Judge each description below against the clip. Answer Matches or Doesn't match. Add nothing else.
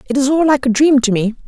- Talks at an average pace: Doesn't match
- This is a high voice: Matches